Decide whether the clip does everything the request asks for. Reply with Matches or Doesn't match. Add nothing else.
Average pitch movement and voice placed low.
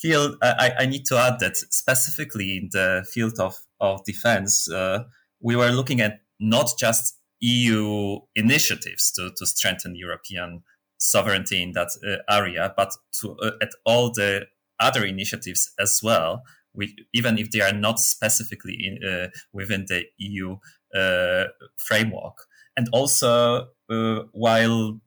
Matches